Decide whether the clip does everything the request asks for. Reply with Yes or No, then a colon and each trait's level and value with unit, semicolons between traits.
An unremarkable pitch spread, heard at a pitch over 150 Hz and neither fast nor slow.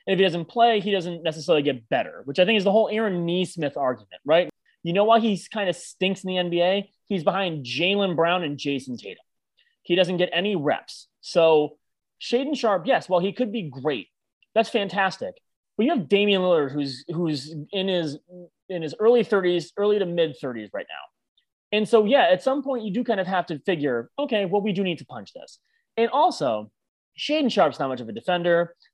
No: average, 4.7 semitones; medium, 185 Hz; fast, 210 wpm